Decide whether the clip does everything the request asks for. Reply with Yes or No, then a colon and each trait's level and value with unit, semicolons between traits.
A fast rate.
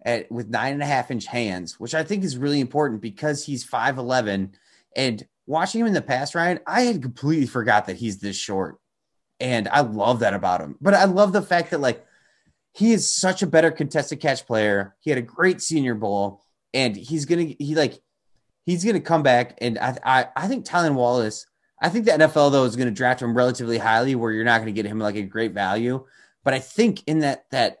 Yes: fast, 220 wpm